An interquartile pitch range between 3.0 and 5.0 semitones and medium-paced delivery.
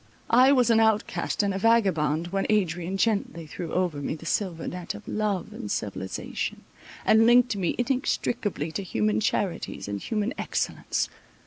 No: wide, 5.6 semitones; average, 155 wpm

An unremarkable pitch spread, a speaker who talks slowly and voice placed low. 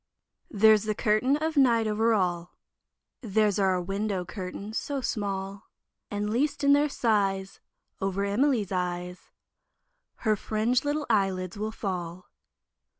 No: average, 3.2 semitones; slow, 130 wpm; high, 210 Hz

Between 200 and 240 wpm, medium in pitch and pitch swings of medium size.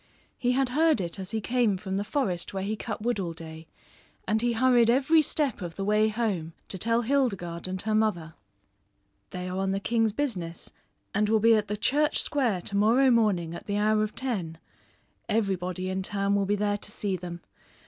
No: fast, 205 wpm; high, 210 Hz; average, 3.9 semitones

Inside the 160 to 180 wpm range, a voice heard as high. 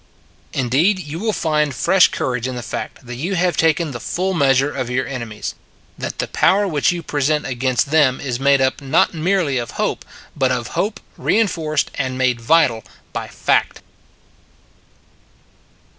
No: average, 170 wpm; medium, 140 Hz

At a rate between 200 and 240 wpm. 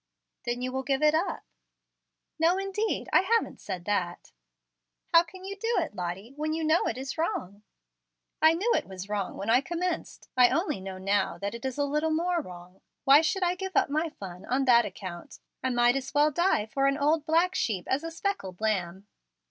Yes: fast, 205 wpm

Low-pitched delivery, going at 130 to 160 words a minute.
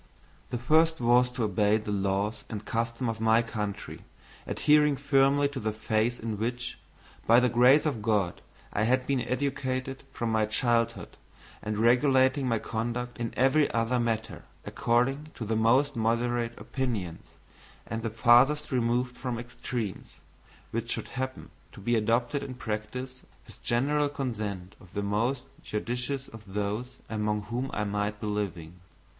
Yes: low, 120 Hz; average, 150 wpm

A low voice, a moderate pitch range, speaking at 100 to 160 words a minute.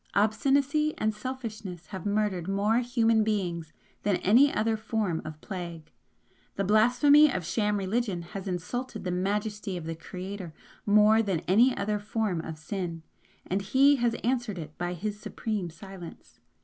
No: high, 205 Hz; average, 3.8 semitones; average, 150 wpm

